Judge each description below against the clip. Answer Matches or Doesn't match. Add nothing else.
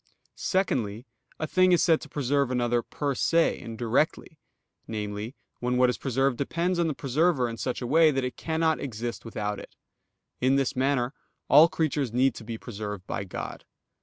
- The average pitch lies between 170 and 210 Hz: Doesn't match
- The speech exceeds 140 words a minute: Matches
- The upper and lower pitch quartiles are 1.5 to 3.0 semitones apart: Doesn't match